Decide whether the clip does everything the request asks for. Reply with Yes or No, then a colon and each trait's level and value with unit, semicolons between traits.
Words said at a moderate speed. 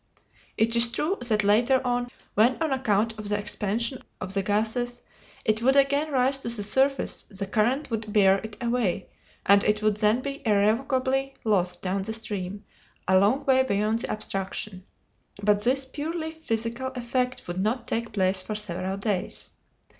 Yes: average, 170 wpm